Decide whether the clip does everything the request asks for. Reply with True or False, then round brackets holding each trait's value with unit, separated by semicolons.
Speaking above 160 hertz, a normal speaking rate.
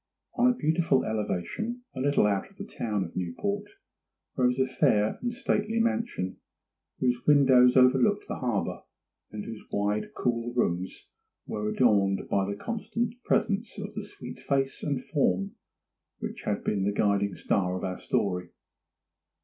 False (125 Hz; 150 wpm)